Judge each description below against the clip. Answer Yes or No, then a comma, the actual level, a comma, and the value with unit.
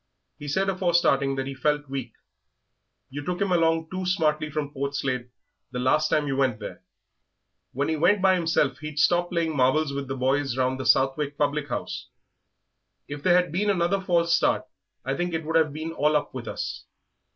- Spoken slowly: No, average, 195 wpm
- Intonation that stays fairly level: No, average, 3.7 semitones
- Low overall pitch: No, medium, 150 Hz